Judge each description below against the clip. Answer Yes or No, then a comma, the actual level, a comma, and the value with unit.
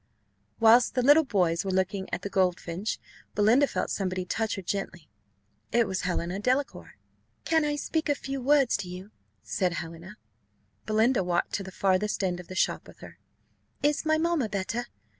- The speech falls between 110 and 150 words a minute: No, average, 175 wpm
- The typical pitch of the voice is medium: No, high, 205 Hz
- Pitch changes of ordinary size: No, wide, 5.7 semitones